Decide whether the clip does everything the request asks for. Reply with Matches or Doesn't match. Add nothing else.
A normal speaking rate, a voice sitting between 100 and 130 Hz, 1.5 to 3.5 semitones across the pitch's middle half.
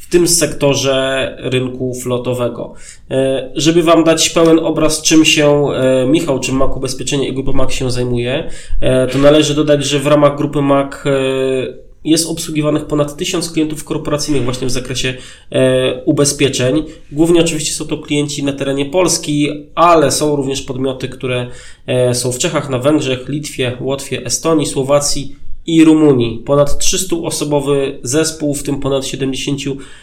Doesn't match